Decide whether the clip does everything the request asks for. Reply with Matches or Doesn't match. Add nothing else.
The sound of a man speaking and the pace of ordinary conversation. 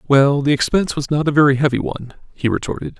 Doesn't match